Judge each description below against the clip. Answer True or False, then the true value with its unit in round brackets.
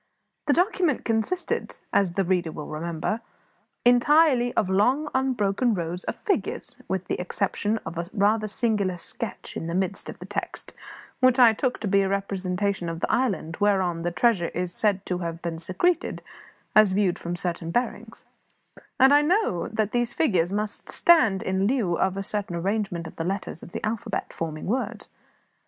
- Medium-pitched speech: False (200 Hz)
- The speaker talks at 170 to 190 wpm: True (175 wpm)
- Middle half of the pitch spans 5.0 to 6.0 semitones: True (5.3 semitones)